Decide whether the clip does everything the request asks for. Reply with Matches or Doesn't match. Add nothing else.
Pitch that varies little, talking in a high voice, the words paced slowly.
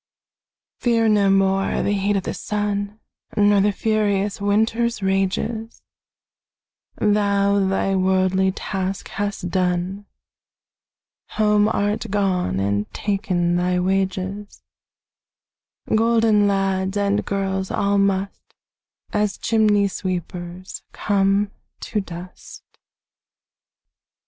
Matches